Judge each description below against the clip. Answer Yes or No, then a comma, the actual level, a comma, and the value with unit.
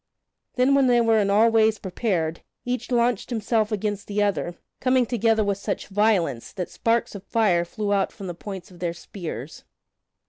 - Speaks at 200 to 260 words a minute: No, average, 180 wpm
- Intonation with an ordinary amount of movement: Yes, average, 3.3 semitones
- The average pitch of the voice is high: Yes, high, 210 Hz